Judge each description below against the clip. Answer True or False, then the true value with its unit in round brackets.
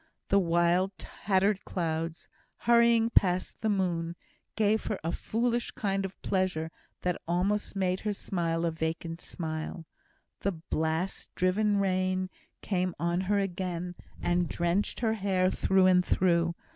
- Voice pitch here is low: False (185 Hz)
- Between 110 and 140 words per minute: True (135 wpm)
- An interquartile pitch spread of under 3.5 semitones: True (2.7 semitones)